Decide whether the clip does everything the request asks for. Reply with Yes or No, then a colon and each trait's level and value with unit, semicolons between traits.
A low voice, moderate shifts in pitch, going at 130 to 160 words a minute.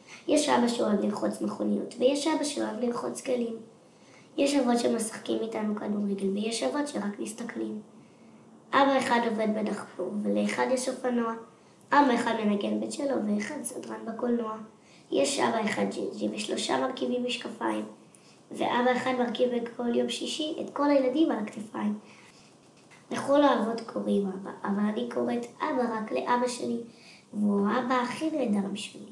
No: high, 230 Hz; average, 3.7 semitones; average, 140 wpm